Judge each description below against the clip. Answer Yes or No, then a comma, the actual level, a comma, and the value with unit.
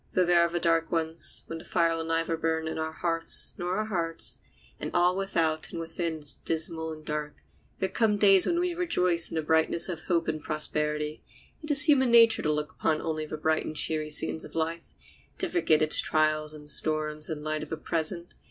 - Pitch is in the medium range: Yes, medium, 165 Hz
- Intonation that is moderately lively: No, narrow, 2.2 semitones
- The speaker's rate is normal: No, fast, 215 wpm